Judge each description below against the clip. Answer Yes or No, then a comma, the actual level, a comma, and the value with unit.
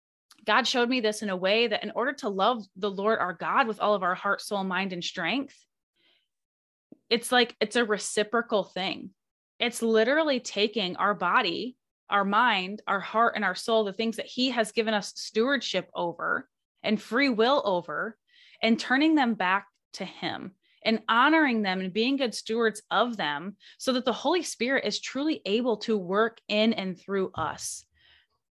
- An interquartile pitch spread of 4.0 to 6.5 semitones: No, average, 3.4 semitones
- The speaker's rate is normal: Yes, average, 180 wpm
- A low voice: No, high, 220 Hz